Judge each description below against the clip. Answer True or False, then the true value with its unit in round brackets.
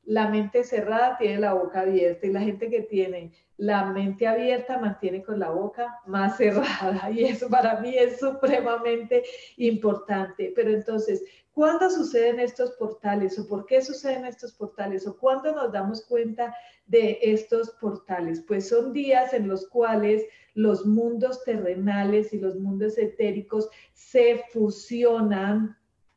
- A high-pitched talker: True (220 Hz)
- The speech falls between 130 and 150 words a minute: True (145 wpm)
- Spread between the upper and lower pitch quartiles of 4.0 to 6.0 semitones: False (3.3 semitones)